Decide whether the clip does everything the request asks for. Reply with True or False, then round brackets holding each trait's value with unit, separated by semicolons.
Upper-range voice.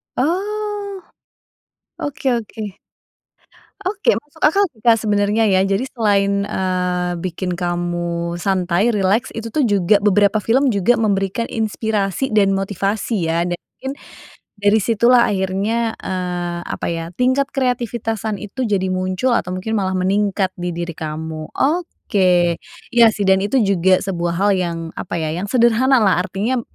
True (200 Hz)